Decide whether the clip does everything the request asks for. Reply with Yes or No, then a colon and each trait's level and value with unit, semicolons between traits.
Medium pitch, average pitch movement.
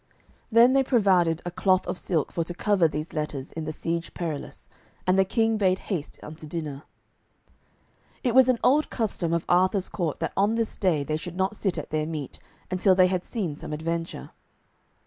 Yes: medium, 180 Hz; average, 4.2 semitones